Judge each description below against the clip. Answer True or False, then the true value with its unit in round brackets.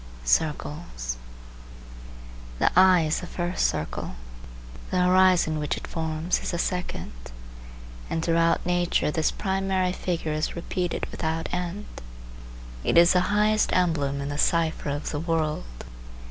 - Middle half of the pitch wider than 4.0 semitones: False (2.8 semitones)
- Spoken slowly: True (130 wpm)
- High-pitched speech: False (170 Hz)